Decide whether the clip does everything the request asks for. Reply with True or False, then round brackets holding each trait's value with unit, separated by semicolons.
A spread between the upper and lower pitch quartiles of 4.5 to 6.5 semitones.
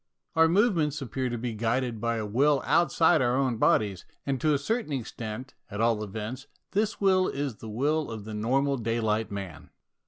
True (4.9 semitones)